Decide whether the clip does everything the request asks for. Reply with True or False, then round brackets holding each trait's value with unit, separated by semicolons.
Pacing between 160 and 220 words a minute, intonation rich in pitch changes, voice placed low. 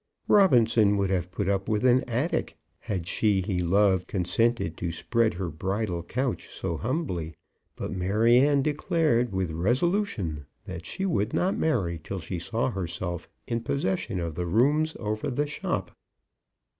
False (150 wpm; 5.8 semitones; 105 Hz)